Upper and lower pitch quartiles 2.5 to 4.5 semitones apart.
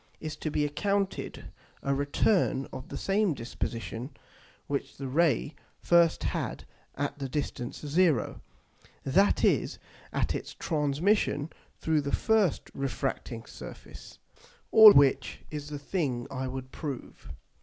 Yes: average, 4.1 semitones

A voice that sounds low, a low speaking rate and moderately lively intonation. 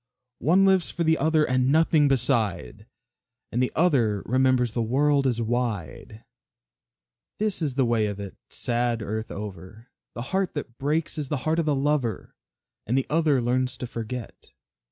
No: low, 130 Hz; average, 165 wpm; average, 4.6 semitones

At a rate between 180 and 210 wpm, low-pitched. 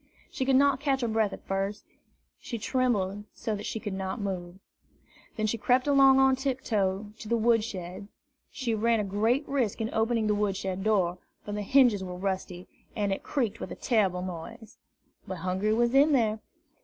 No: average, 195 wpm; high, 215 Hz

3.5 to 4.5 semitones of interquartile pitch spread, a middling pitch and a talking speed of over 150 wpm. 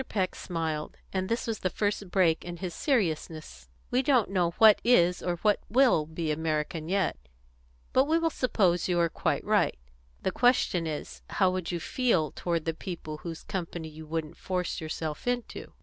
Yes: average, 4.1 semitones; medium, 175 Hz; average, 175 wpm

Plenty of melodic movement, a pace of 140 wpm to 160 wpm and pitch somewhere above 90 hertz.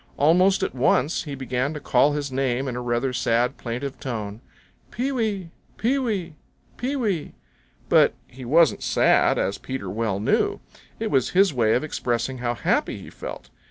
No: wide, 5.7 semitones; average, 170 wpm; low, 135 Hz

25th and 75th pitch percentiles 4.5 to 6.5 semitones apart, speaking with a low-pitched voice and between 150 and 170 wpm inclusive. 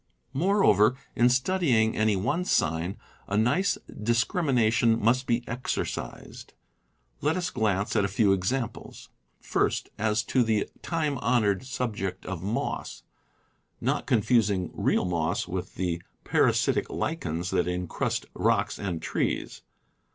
No: average, 4.8 semitones; low, 110 Hz; slow, 135 wpm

